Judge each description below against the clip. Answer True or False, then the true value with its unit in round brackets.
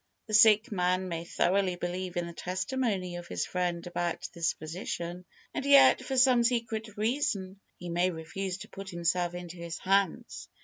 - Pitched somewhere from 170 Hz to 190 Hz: True (185 Hz)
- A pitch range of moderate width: True (3.3 semitones)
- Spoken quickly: False (170 wpm)